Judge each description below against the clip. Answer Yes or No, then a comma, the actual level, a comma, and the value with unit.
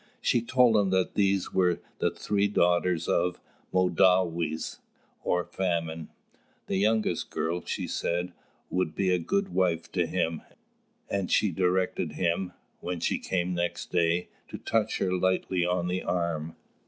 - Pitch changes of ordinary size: No, narrow, 1.7 semitones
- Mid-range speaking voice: No, very low, 90 Hz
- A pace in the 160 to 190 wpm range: No, average, 145 wpm